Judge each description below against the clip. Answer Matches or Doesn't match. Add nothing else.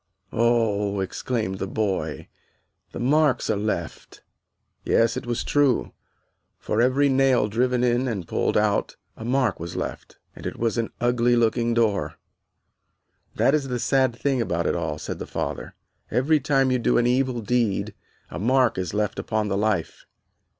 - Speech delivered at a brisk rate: Doesn't match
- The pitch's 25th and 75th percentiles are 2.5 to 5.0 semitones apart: Matches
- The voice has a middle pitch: Doesn't match